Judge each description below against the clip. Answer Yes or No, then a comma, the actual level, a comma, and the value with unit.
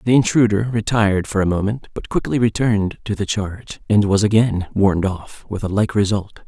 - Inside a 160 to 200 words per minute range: Yes, average, 195 wpm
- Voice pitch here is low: Yes, low, 105 Hz